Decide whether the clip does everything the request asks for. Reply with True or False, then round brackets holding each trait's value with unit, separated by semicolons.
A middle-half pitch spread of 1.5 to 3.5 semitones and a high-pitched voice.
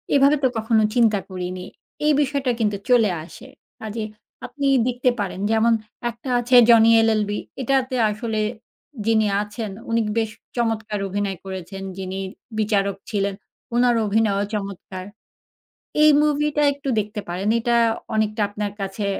True (3.1 semitones; 220 Hz)